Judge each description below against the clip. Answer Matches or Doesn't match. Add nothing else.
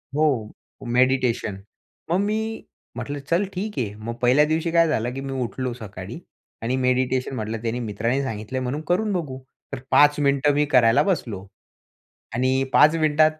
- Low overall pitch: Matches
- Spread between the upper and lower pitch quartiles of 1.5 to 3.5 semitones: Doesn't match